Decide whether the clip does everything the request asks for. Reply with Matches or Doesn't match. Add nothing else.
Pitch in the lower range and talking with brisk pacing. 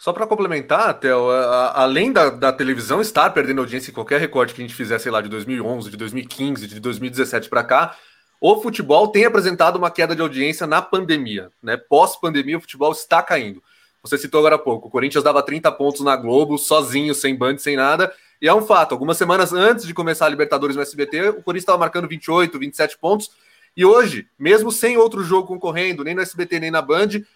Doesn't match